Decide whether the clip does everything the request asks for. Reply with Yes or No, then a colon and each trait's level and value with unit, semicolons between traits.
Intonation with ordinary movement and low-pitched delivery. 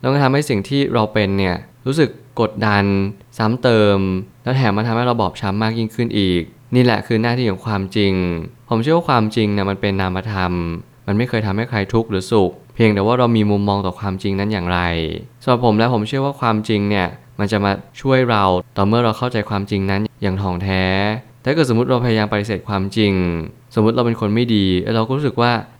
Yes: average, 3.5 semitones; low, 110 Hz